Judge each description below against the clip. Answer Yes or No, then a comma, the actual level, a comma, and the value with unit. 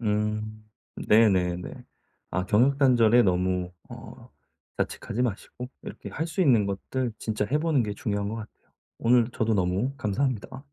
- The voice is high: No, low, 110 Hz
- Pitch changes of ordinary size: Yes, average, 3.7 semitones